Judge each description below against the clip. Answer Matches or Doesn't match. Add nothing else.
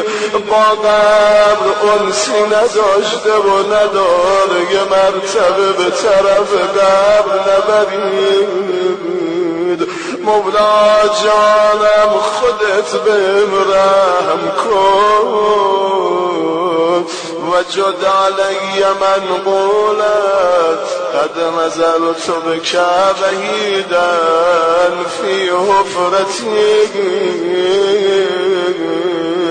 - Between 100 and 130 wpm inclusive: Doesn't match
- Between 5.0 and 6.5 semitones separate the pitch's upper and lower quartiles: Doesn't match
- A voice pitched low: Doesn't match